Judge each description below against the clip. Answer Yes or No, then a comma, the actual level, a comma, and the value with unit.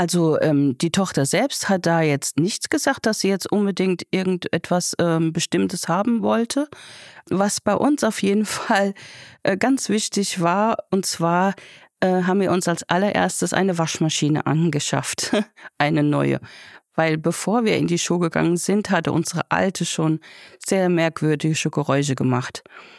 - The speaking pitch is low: No, medium, 175 Hz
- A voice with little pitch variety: No, average, 3.9 semitones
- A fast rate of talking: No, average, 150 wpm